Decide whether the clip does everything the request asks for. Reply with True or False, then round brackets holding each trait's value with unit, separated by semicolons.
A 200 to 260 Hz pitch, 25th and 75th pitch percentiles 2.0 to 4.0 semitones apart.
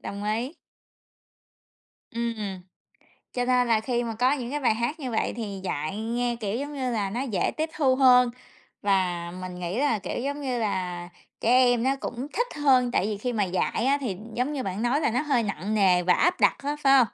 False (240 Hz; 4.5 semitones)